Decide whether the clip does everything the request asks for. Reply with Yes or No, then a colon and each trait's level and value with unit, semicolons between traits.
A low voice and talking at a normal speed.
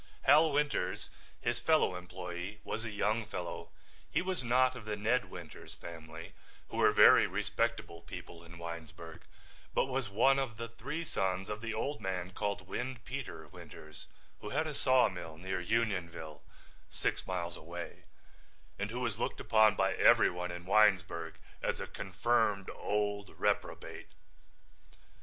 Yes: low, 105 Hz; average, 145 wpm